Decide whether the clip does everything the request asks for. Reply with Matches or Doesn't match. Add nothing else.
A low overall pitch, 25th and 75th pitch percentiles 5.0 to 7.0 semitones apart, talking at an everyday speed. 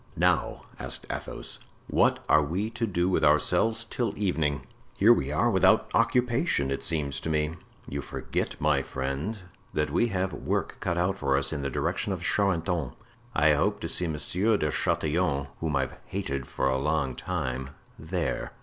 Matches